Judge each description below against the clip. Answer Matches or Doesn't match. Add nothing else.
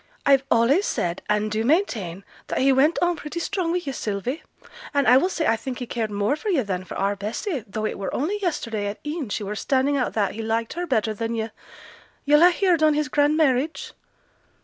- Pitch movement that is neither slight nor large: Doesn't match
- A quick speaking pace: Matches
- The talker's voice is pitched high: Matches